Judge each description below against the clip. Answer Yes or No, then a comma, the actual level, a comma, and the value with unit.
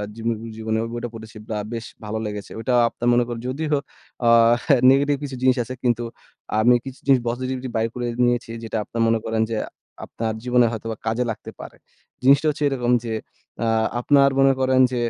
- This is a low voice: Yes, low, 120 Hz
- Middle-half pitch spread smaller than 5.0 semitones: Yes, narrow, 2.5 semitones